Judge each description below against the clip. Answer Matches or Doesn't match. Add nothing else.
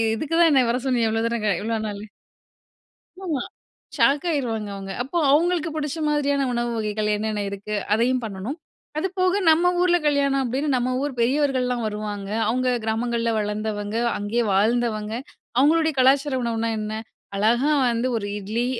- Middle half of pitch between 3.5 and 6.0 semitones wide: Matches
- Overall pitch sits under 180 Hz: Doesn't match